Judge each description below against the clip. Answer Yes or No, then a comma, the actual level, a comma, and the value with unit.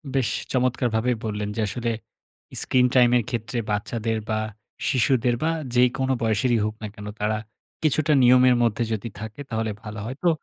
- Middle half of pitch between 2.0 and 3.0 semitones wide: Yes, narrow, 2.5 semitones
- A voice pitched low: Yes, low, 120 Hz